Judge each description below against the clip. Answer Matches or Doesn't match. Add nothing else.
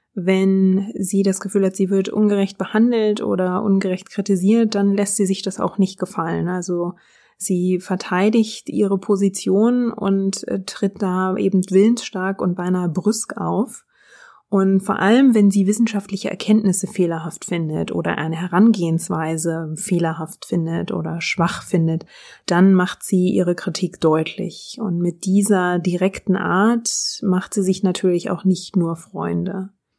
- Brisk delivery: Doesn't match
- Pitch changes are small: Matches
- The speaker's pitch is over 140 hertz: Matches